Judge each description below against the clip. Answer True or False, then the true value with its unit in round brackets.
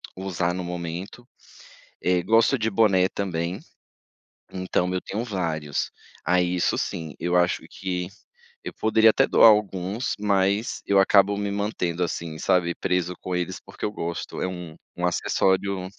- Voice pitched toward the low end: True (95 Hz)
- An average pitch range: False (2.3 semitones)